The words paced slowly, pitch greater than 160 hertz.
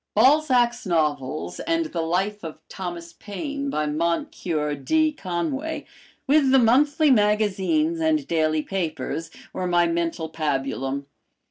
Yes: slow, 120 wpm; medium, 185 Hz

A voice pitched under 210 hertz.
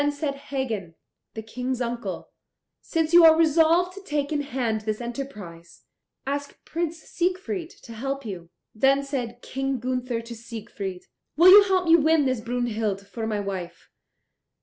No: very high, 255 Hz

